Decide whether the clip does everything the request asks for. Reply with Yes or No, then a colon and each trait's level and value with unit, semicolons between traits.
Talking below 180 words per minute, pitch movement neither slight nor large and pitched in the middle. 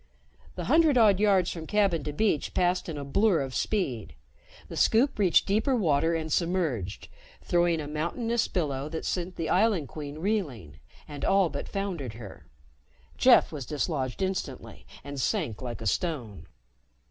No: average, 160 wpm; wide, 5.8 semitones; medium, 165 Hz